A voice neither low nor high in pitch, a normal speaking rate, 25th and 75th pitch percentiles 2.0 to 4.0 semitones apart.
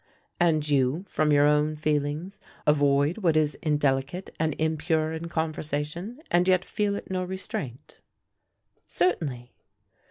No: medium, 155 Hz; slow, 125 wpm; average, 3.2 semitones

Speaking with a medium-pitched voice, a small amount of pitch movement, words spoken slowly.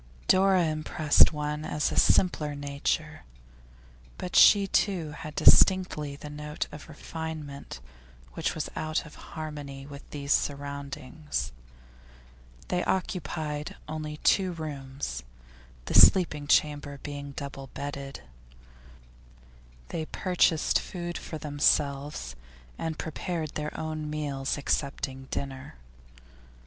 Yes: medium, 150 Hz; narrow, 2.0 semitones; slow, 105 wpm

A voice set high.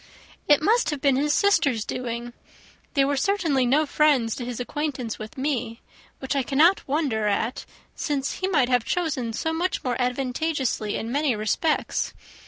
Yes: very high, 270 Hz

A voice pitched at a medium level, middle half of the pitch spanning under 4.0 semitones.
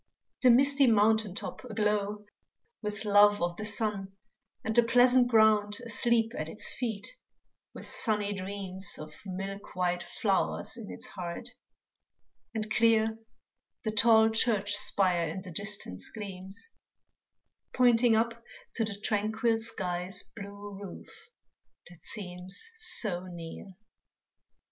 No: high, 210 Hz; average, 2.8 semitones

